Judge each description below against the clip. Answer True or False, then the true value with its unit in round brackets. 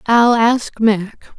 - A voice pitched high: True (225 Hz)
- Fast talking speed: False (130 wpm)